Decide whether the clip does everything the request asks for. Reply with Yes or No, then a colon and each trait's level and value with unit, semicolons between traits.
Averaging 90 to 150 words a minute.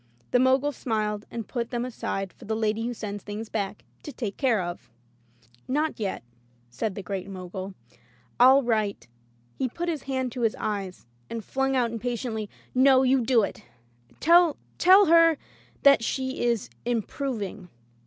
No: average, 175 wpm